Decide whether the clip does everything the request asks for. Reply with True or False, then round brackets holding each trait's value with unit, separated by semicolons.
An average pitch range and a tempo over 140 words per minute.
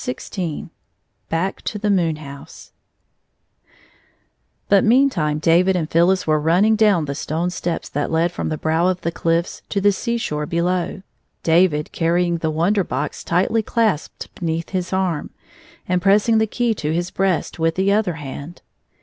True (3.3 semitones; 170 wpm)